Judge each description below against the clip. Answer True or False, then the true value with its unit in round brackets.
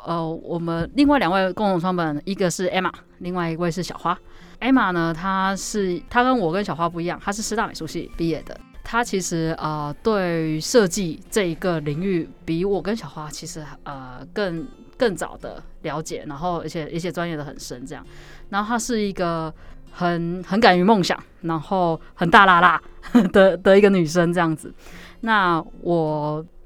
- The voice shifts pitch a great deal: False (3.3 semitones)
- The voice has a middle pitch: True (175 Hz)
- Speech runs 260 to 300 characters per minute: True (270 characters per minute)